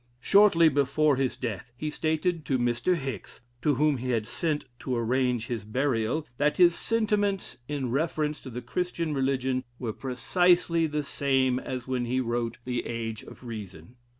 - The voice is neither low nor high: No, low, 130 Hz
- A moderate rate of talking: Yes, average, 165 wpm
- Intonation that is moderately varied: Yes, average, 4.2 semitones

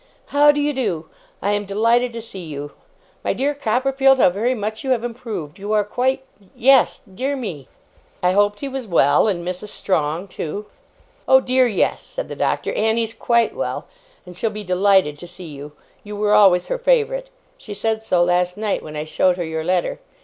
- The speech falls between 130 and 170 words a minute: No, average, 195 wpm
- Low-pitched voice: No, high, 210 Hz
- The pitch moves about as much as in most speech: No, wide, 5.9 semitones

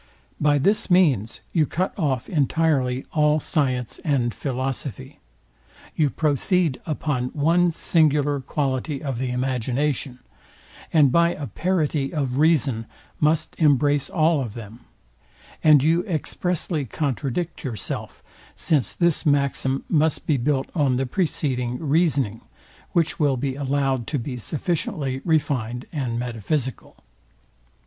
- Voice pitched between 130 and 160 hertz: Yes, medium, 140 Hz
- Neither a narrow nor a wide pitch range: Yes, average, 3.4 semitones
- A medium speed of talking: No, slow, 120 wpm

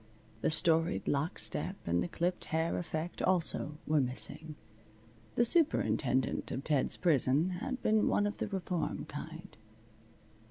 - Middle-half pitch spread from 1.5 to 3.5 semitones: No, average, 4.0 semitones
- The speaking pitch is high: No, medium, 165 Hz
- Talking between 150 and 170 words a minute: No, slow, 135 wpm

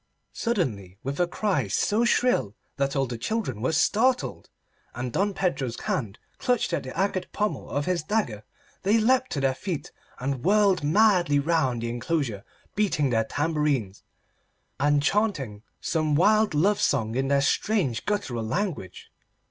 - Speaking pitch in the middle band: Yes, medium, 150 Hz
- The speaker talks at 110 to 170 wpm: Yes, average, 150 wpm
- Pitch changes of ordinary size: No, wide, 8.3 semitones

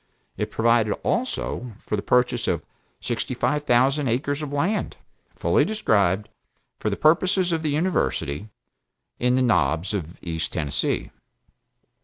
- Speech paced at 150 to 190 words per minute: No, slow, 135 wpm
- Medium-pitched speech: No, low, 125 Hz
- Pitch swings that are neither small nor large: No, wide, 7.3 semitones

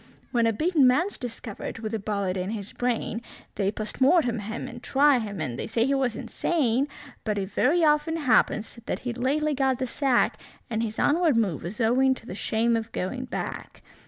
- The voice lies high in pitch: Yes, high, 240 Hz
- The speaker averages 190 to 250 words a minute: Yes, average, 200 wpm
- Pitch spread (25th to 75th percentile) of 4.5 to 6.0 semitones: No, average, 3.9 semitones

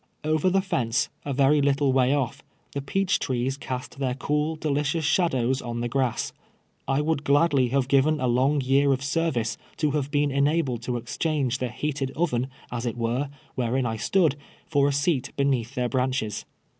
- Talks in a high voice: No, low, 135 Hz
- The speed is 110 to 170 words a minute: No, average, 185 wpm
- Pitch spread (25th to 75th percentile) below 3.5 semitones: Yes, average, 2.9 semitones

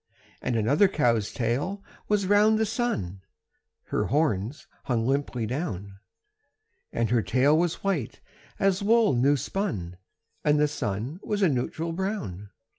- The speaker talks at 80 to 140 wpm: Yes, slow, 135 wpm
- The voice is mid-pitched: Yes, medium, 145 Hz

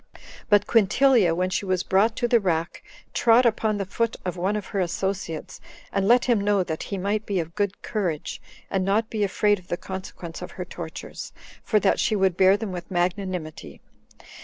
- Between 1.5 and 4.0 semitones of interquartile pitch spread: Yes, average, 2.7 semitones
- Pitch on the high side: Yes, high, 195 Hz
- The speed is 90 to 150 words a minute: No, average, 195 wpm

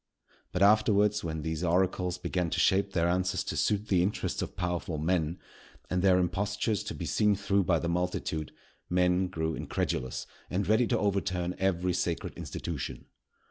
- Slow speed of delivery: No, average, 165 wpm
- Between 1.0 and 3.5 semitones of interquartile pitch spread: Yes, narrow, 2.4 semitones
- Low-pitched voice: Yes, very low, 90 Hz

